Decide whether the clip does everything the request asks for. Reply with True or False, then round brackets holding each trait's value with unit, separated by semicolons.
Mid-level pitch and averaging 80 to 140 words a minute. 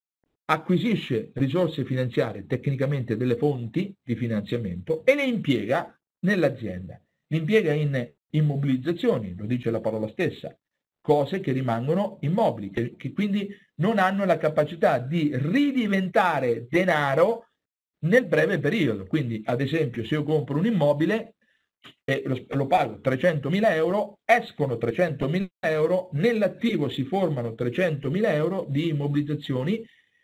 True (155 Hz; 125 wpm)